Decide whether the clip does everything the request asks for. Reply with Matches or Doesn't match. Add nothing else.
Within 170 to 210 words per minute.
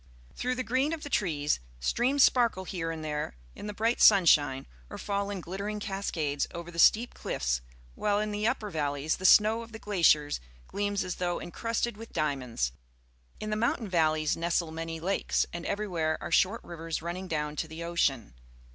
Matches